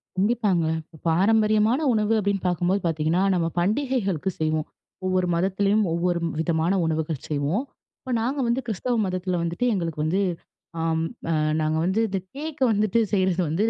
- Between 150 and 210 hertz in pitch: Yes, medium, 185 Hz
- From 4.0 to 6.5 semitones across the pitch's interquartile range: Yes, average, 4.4 semitones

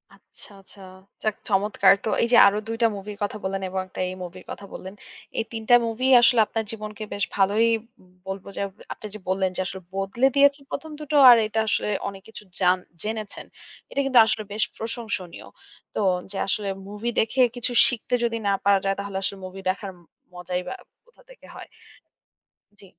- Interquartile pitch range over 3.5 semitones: No, average, 2.9 semitones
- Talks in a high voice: Yes, high, 210 Hz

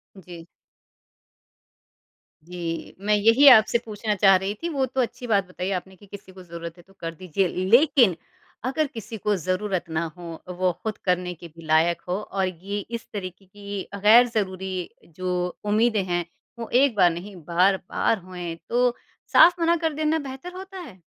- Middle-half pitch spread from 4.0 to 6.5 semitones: Yes, average, 4.6 semitones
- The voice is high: Yes, high, 195 Hz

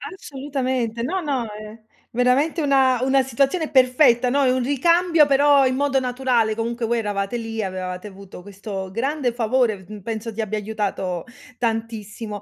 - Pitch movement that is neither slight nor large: Yes, average, 3.9 semitones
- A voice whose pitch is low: No, high, 240 Hz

